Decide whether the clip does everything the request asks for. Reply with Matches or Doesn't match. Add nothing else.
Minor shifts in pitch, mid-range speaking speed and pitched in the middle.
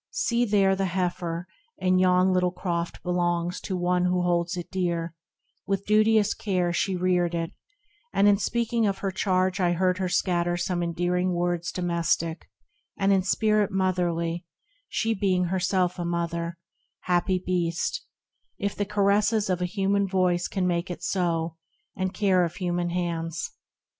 Matches